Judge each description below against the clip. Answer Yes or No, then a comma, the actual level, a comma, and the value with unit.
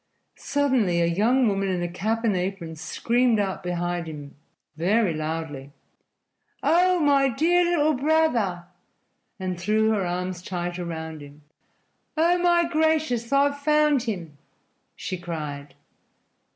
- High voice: Yes, high, 195 Hz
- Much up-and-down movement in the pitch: Yes, wide, 8.6 semitones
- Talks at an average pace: No, slow, 125 wpm